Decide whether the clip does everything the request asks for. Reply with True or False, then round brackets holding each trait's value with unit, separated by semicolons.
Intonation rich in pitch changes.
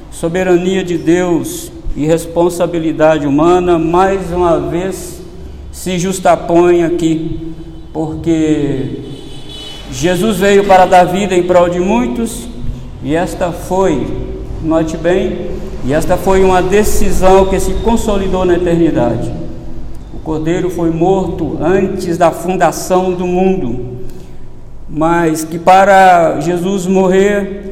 False (2.7 semitones)